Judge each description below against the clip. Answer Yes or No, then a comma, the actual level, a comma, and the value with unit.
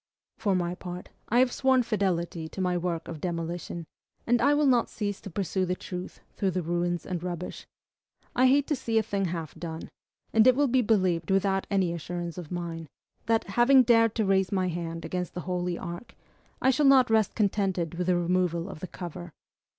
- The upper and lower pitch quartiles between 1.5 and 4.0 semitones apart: No, average, 4.4 semitones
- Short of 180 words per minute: No, average, 200 wpm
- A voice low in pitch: No, medium, 185 Hz